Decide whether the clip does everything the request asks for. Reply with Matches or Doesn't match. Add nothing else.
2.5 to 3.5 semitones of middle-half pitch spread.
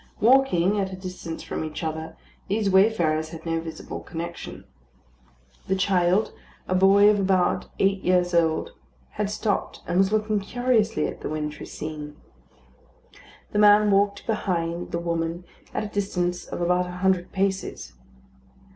Matches